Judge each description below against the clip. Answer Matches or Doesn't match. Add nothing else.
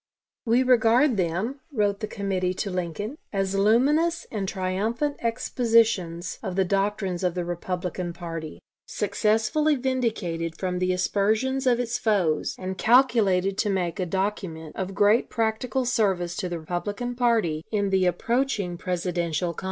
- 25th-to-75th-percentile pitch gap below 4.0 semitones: Doesn't match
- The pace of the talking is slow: Doesn't match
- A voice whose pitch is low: Doesn't match